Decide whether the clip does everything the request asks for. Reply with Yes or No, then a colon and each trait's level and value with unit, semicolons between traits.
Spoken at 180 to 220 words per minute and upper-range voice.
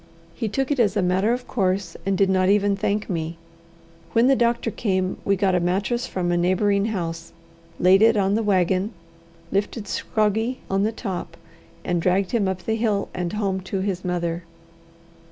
Yes: average, 185 wpm; high, 195 Hz